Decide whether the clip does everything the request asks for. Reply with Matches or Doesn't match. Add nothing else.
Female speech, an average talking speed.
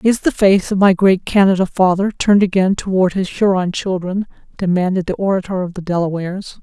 Matches